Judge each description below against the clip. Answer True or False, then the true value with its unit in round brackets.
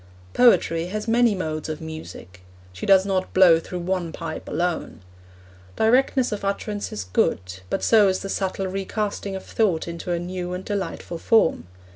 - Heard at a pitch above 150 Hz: True (185 Hz)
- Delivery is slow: False (165 wpm)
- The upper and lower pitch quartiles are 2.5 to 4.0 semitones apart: True (3.6 semitones)